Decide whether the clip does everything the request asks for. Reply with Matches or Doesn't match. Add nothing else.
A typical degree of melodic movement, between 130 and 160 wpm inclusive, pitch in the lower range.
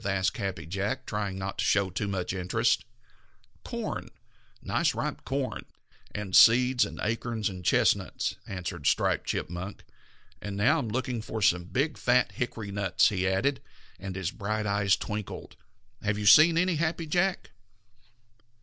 Matches